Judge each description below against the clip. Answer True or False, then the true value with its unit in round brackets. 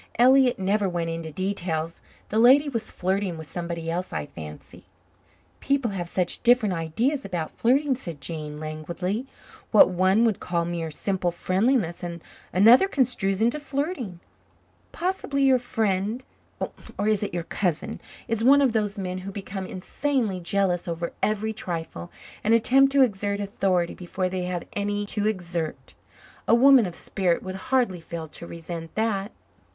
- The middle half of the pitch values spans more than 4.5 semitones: True (5.1 semitones)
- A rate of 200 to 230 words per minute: False (155 wpm)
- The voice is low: False (195 Hz)